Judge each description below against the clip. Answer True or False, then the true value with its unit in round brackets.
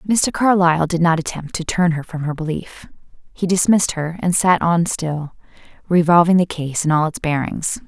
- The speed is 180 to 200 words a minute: True (190 wpm)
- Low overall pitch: False (170 Hz)